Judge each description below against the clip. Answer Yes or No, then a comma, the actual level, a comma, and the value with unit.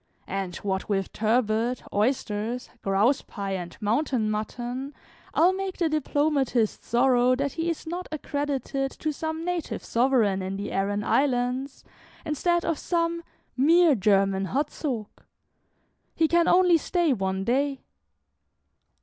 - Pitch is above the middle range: Yes, very high, 255 Hz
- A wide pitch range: Yes, wide, 6.6 semitones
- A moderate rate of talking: No, slow, 130 wpm